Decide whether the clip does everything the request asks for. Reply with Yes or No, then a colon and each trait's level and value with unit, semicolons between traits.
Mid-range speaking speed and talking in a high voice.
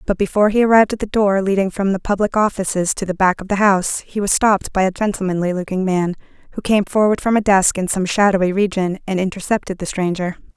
No: fast, 225 wpm; high, 195 Hz